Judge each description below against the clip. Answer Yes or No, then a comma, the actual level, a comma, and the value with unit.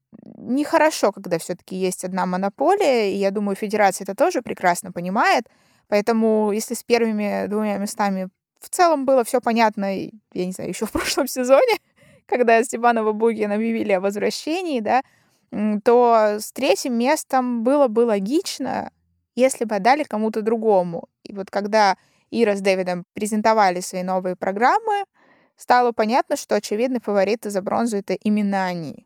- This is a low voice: No, high, 215 Hz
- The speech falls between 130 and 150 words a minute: Yes, average, 145 wpm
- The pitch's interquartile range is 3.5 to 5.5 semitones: Yes, average, 4.2 semitones